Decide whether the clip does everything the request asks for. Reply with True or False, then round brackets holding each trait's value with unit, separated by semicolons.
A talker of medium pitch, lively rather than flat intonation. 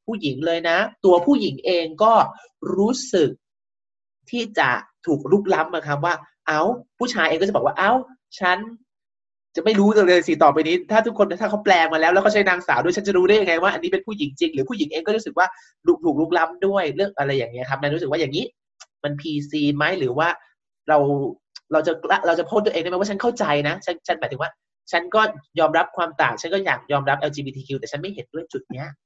True (170 Hz; 5.8 semitones)